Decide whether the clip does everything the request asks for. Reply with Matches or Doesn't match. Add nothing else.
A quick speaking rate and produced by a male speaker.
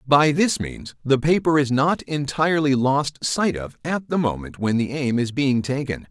Doesn't match